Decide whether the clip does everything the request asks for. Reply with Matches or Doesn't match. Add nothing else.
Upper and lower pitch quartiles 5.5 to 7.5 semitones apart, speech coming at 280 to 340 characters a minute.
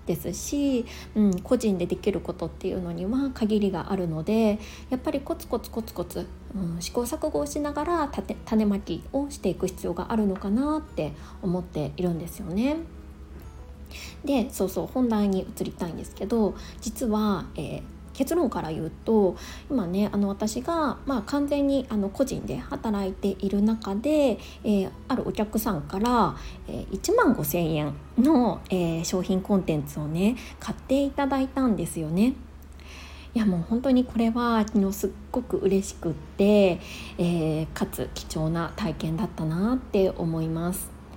Matches